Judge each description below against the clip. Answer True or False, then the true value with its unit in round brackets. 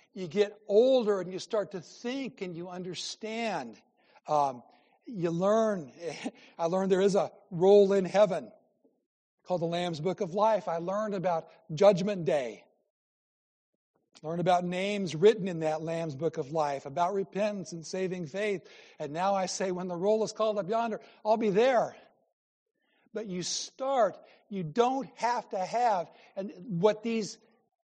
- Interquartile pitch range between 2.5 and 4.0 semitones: True (3.6 semitones)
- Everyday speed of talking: True (155 wpm)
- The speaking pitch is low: False (195 Hz)